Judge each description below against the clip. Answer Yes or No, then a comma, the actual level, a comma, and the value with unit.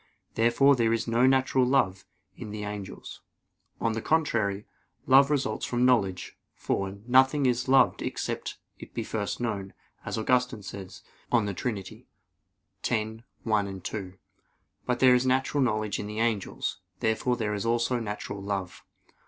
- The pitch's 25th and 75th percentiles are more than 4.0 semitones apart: No, average, 3.5 semitones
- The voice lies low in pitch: Yes, low, 115 Hz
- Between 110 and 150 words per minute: Yes, average, 145 wpm